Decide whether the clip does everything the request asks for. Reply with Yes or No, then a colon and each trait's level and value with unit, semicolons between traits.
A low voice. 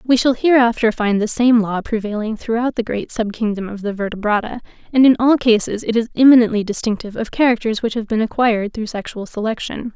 No: high, 225 Hz